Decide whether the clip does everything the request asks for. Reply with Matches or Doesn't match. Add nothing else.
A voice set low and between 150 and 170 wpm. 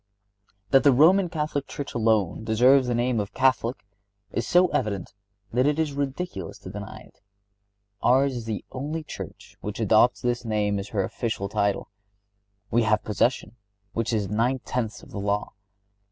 Matches